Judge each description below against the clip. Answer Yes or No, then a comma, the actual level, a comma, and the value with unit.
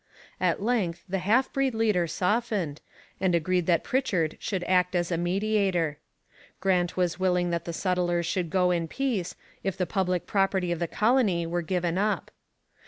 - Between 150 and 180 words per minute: Yes, average, 170 wpm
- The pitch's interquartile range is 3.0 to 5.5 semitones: No, narrow, 2.4 semitones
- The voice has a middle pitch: Yes, medium, 180 Hz